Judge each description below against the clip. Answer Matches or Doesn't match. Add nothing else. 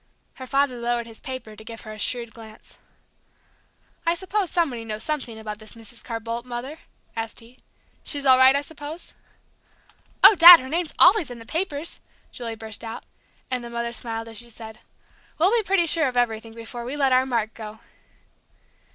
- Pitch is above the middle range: Matches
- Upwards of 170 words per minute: Matches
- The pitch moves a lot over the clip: Doesn't match